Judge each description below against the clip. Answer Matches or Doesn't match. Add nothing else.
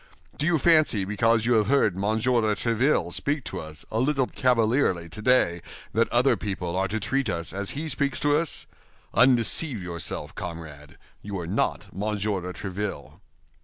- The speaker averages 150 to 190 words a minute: Matches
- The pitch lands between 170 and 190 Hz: Doesn't match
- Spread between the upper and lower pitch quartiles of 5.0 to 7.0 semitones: Matches